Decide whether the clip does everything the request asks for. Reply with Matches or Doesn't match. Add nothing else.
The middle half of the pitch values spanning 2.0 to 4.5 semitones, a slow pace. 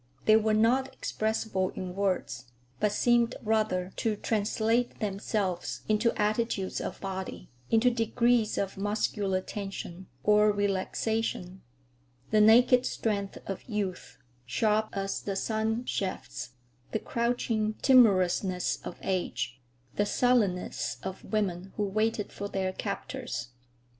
Matches